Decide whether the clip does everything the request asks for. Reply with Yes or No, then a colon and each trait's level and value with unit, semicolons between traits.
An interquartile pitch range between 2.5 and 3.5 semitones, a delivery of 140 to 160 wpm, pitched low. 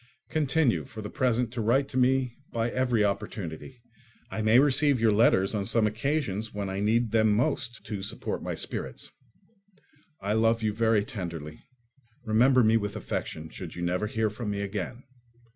No: average, 3.2 semitones; average, 170 wpm; low, 110 Hz